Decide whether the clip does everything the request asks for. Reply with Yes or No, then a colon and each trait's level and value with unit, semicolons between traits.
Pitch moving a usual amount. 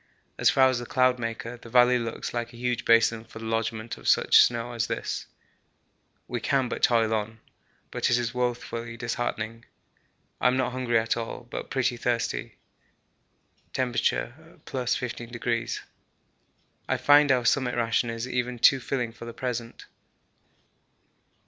No: narrow, 1.4 semitones